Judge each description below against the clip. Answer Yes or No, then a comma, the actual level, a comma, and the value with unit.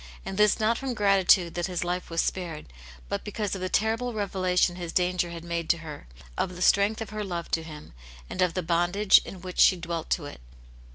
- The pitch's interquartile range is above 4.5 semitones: No, average, 2.9 semitones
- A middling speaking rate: No, fast, 220 wpm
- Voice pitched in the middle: Yes, medium, 180 Hz